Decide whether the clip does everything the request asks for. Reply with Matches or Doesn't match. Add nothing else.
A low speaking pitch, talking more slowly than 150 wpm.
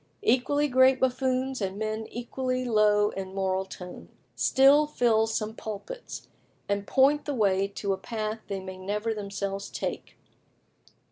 Doesn't match